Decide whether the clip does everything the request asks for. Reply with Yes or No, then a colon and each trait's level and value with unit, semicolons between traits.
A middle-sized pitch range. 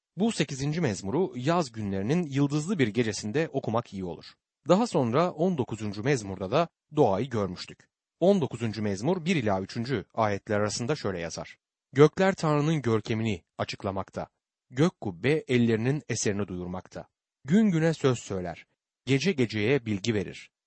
No: wide, 7.1 semitones